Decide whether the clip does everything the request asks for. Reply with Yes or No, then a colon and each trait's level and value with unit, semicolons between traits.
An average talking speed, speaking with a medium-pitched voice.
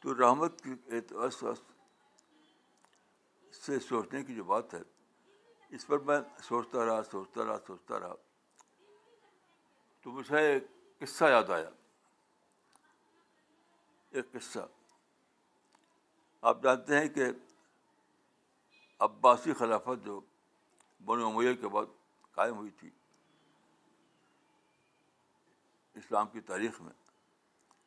No: slow, 95 wpm; medium, 145 Hz